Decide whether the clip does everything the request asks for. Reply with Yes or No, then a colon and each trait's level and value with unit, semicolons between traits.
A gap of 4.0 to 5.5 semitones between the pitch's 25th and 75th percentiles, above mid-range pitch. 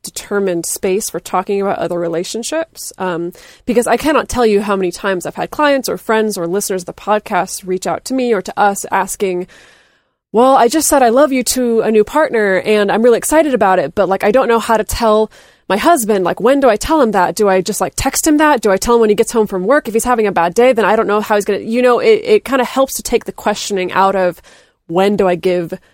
Yes: average, 4.4 semitones; high, 215 Hz